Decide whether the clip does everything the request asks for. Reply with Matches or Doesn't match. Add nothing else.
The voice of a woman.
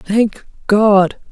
Matches